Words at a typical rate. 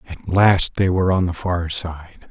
No: fast, 210 wpm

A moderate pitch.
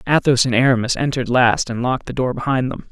No: low, 125 Hz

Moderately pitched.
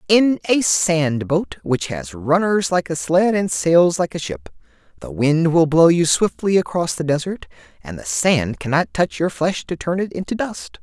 Yes: medium, 160 Hz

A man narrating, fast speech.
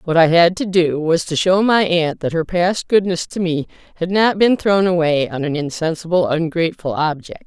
No: female; fast, 210 wpm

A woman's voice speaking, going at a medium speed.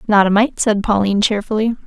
Yes: female; average, 195 wpm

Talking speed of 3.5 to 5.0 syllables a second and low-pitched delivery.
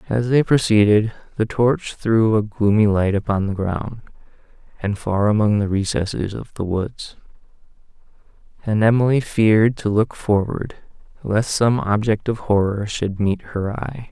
Yes: 4.4 syllables/s; low, 110 Hz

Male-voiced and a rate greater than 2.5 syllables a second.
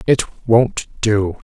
No: male; 2.3 syllables/s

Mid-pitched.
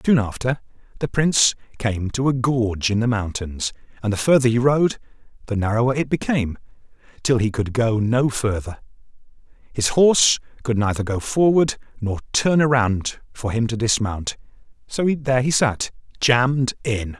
No: low, 120 Hz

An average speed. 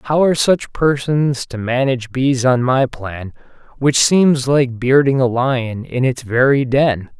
Yes: average, 165 wpm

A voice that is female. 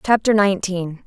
Yes: female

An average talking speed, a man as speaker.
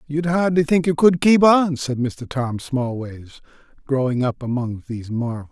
Yes: average, 175 wpm; male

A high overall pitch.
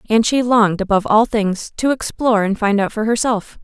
Yes: high, 215 Hz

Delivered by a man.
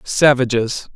Yes: male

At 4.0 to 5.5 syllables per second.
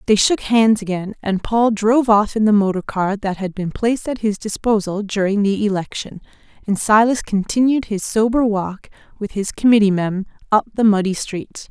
Yes: 5.0 syllables/s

